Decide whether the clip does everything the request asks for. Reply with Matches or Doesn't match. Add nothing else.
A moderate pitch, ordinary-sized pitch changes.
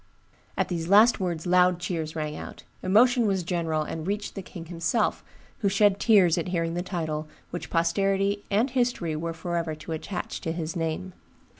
Matches